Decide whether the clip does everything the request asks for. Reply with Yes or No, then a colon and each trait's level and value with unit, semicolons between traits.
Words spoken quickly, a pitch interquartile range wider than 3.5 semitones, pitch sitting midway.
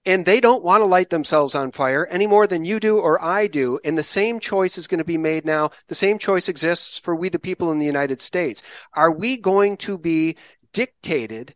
Yes: fast, 235 wpm; average, 4.3 semitones; medium, 175 Hz